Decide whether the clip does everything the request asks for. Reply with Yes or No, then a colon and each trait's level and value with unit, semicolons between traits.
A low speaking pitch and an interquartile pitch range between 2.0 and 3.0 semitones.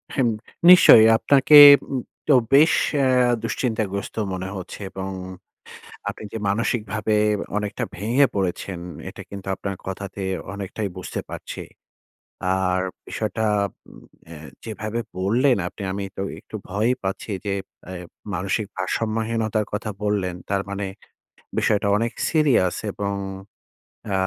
Yes: low, 105 Hz; average, 2.7 semitones